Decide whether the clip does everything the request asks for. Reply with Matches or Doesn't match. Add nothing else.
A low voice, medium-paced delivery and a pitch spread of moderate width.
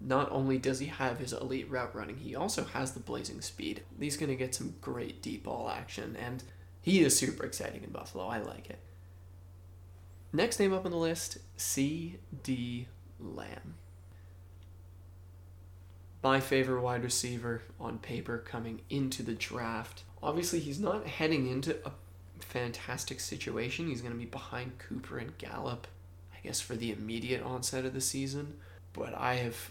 Doesn't match